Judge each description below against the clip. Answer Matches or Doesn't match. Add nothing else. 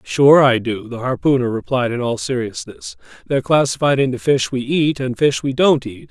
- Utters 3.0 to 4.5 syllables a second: Doesn't match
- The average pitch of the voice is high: Doesn't match